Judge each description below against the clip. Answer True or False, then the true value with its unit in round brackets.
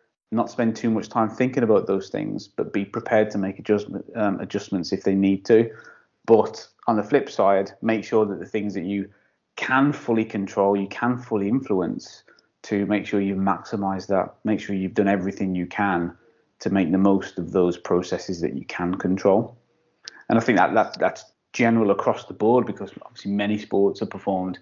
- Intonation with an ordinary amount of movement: False (2.2 semitones)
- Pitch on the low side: True (100 Hz)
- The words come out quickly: False (195 wpm)